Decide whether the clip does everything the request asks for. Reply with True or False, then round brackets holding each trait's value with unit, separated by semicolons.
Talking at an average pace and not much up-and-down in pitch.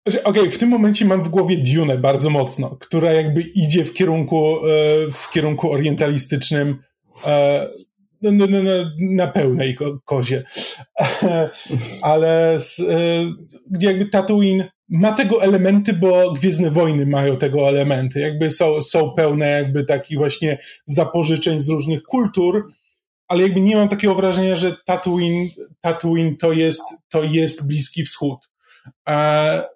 False (125 wpm; 4.1 semitones)